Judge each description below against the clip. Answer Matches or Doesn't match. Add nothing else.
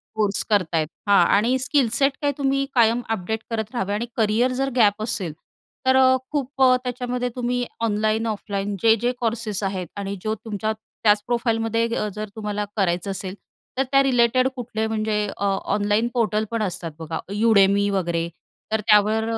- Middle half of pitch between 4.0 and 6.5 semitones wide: Doesn't match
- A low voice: Doesn't match